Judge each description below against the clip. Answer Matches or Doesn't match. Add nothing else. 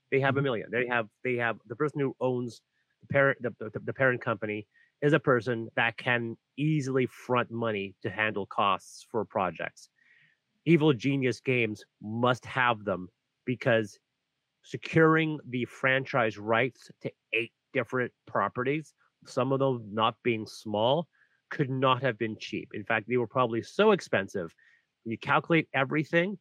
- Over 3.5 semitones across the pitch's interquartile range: Doesn't match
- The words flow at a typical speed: Matches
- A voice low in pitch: Matches